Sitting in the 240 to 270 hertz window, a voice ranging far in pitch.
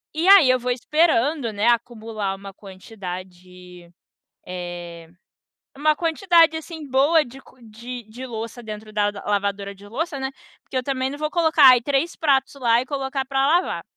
Yes: high, 245 Hz; wide, 5.9 semitones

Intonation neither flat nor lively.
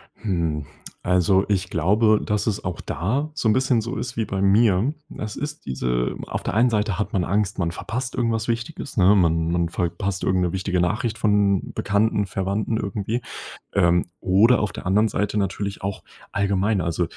Yes: average, 3.3 semitones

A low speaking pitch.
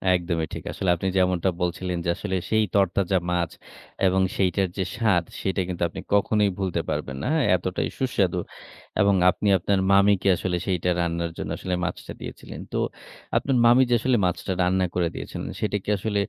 Yes: very low, 95 Hz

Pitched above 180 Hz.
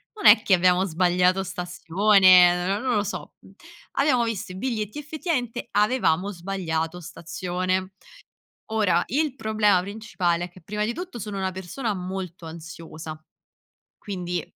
Yes: high, 190 Hz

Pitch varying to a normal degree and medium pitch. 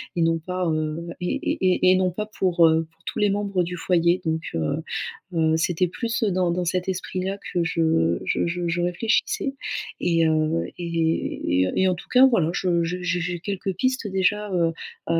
No: narrow, 2.2 semitones; medium, 175 Hz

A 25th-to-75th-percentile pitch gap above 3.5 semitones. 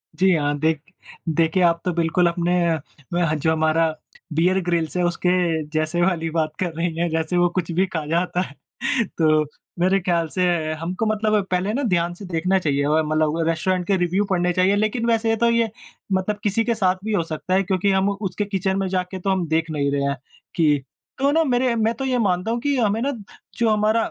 Yes: average, 4.1 semitones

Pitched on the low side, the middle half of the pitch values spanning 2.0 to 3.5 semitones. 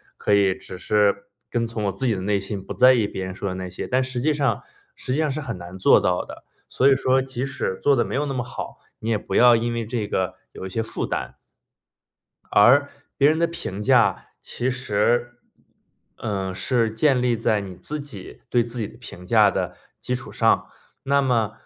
No: low, 115 Hz; average, 4.3 semitones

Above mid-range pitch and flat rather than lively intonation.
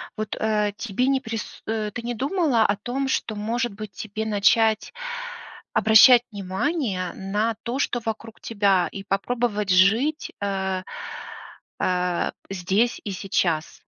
No: high, 215 Hz; average, 3.3 semitones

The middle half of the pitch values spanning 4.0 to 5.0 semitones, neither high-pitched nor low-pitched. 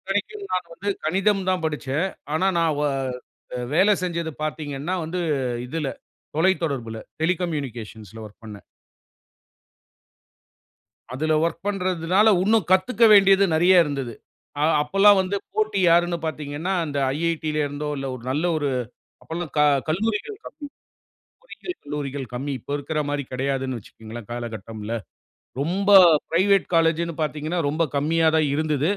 Yes: average, 4.6 semitones; medium, 160 Hz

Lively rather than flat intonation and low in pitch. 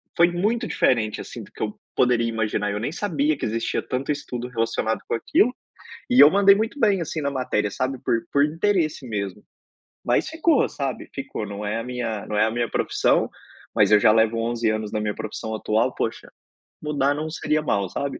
Yes: wide, 5.8 semitones; low, 125 Hz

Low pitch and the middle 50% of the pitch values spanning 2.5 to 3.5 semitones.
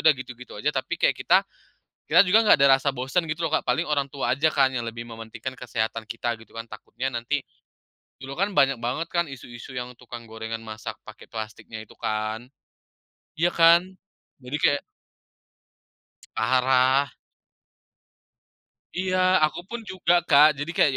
No: low, 130 Hz; average, 4.4 semitones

